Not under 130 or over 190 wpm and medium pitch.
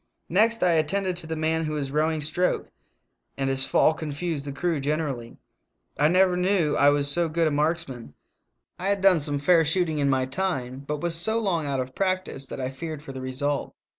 No: fast, 205 wpm; medium, 155 Hz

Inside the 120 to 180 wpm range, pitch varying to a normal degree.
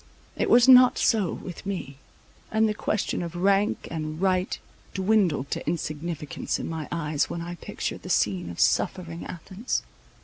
Yes: average, 160 wpm; average, 4.3 semitones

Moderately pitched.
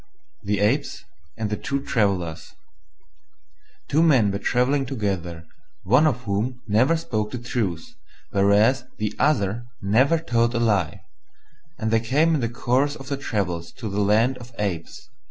No: low, 115 Hz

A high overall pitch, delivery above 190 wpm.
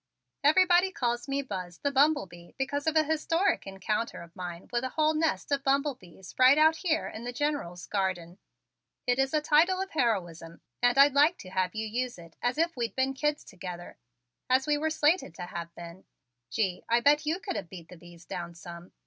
Yes: very high, 250 Hz; fast, 205 wpm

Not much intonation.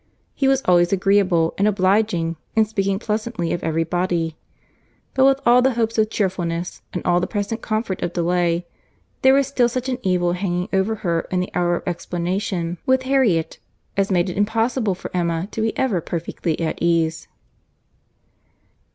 No: average, 4.2 semitones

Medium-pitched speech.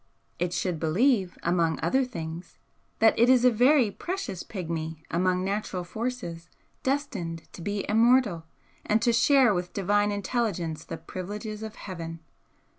No: high, 200 Hz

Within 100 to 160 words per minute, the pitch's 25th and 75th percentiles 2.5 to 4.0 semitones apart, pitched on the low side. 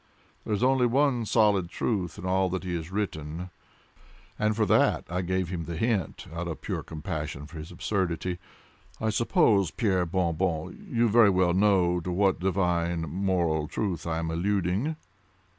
No: average, 170 wpm; average, 3.5 semitones; very low, 90 Hz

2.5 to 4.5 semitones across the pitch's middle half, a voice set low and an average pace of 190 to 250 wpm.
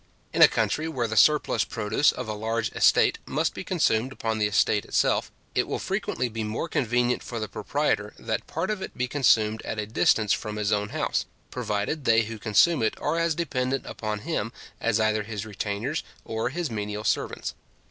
Yes: average, 3.5 semitones; low, 110 Hz; average, 195 wpm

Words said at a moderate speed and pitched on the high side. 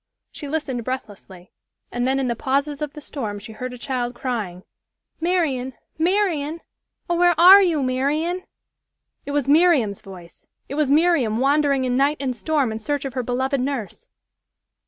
Yes: average, 165 wpm; very high, 275 Hz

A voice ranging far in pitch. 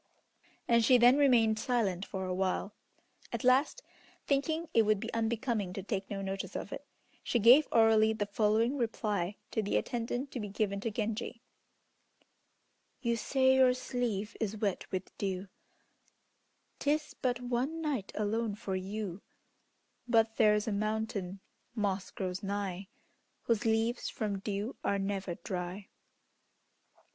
No: average, 3.3 semitones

